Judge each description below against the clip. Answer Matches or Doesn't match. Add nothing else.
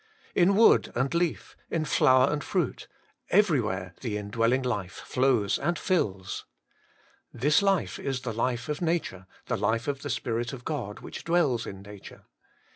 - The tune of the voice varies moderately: Doesn't match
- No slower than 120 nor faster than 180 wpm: Matches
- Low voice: Matches